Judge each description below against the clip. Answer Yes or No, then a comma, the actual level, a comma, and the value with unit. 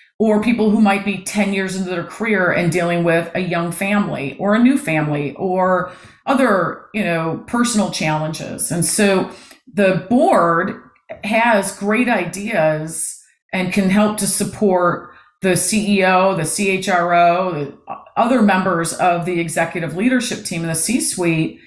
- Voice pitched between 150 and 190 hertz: Yes, medium, 185 Hz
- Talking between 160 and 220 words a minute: No, average, 145 wpm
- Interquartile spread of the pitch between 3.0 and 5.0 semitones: Yes, average, 3.4 semitones